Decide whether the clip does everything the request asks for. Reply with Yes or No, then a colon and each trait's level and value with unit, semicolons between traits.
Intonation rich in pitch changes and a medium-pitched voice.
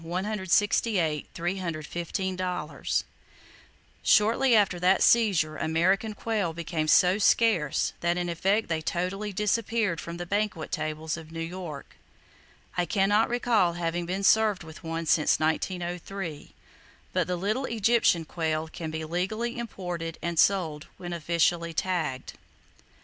No: average, 4.0 semitones; medium, 175 Hz